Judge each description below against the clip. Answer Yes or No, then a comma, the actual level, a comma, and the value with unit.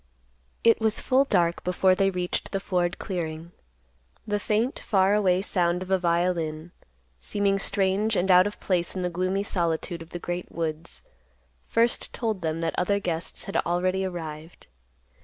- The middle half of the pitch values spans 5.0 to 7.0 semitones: No, narrow, 2.5 semitones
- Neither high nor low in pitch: Yes, medium, 180 Hz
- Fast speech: No, average, 160 wpm